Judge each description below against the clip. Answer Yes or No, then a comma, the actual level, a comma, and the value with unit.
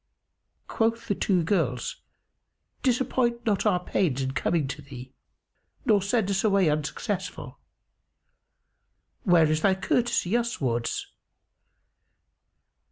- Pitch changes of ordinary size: No, wide, 7.1 semitones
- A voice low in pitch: No, high, 190 Hz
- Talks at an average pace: No, slow, 100 wpm